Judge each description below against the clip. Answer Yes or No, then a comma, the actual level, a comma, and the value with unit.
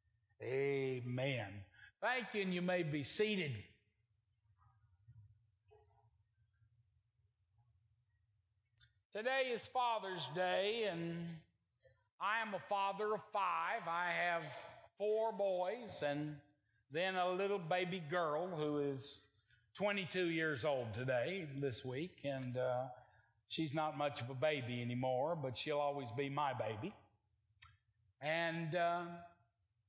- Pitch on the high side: No, medium, 140 Hz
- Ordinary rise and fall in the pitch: No, wide, 7.7 semitones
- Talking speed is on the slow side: Yes, slow, 110 wpm